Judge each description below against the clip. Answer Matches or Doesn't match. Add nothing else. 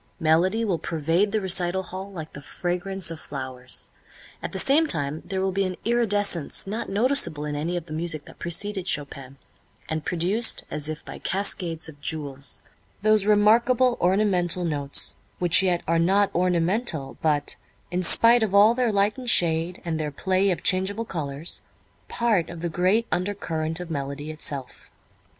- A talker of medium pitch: Matches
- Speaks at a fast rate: Doesn't match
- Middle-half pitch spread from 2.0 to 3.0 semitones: Doesn't match